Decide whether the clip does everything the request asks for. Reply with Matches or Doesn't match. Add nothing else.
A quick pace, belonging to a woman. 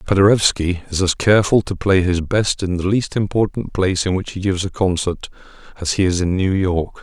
Doesn't match